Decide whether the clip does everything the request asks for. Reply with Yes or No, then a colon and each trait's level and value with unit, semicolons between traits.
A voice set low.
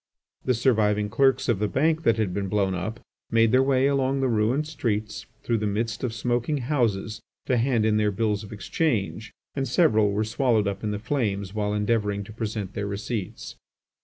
Yes: low, 110 Hz